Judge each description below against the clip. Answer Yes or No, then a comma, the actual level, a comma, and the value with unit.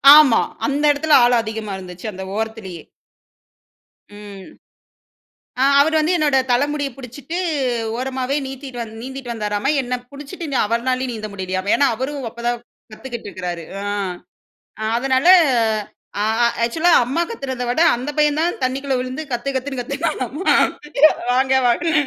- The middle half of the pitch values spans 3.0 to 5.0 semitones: Yes, average, 3.9 semitones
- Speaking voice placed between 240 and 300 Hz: Yes, very high, 255 Hz